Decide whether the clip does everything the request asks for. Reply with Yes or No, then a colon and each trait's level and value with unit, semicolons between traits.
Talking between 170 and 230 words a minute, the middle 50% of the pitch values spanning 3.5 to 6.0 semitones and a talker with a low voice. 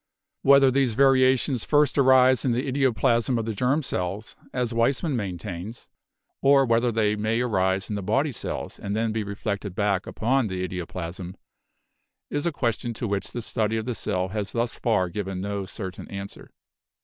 Yes: average, 175 wpm; average, 4.4 semitones; low, 110 Hz